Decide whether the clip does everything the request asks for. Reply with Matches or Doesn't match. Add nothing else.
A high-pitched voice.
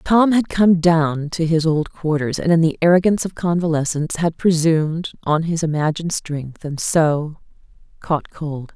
Doesn't match